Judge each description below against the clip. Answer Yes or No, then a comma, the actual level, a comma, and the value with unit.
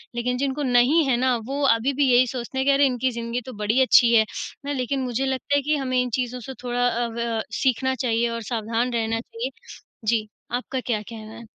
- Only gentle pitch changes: Yes, narrow, 2.2 semitones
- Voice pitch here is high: Yes, high, 245 Hz